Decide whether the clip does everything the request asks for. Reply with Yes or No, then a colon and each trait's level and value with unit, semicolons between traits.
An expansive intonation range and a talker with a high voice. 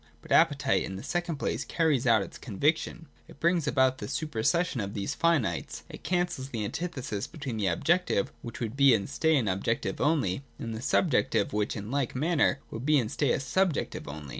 No: wide, 6.7 semitones; low, 130 Hz